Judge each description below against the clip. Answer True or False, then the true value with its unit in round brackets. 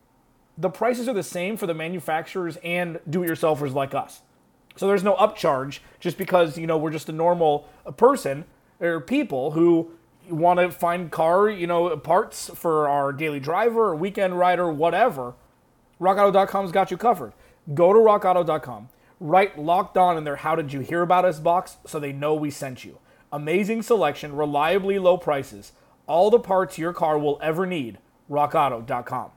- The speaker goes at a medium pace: True (170 wpm)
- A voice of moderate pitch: True (170 Hz)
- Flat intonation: False (3.6 semitones)